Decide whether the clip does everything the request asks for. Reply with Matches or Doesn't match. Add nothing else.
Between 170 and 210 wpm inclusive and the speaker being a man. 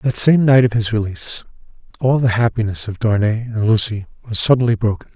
Matches